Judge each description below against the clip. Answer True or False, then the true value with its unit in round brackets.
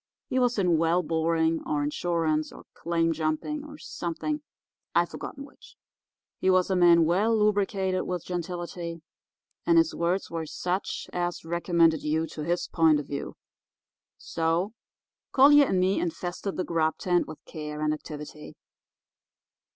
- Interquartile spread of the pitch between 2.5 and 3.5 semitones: True (2.8 semitones)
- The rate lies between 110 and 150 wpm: True (145 wpm)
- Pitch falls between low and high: True (170 Hz)